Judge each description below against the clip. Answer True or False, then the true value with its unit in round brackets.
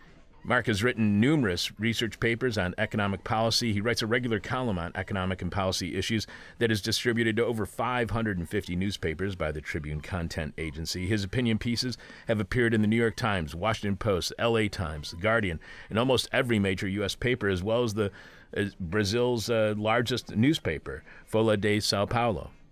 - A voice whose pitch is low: True (110 Hz)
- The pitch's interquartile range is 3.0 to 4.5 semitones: True (3.5 semitones)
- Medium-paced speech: True (175 wpm)